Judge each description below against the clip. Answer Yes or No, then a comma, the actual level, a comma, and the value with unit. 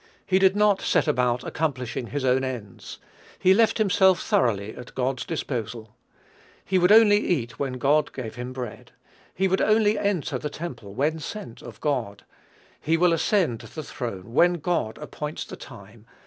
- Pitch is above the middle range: No, medium, 140 Hz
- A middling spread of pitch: No, wide, 7.1 semitones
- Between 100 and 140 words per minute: No, average, 165 wpm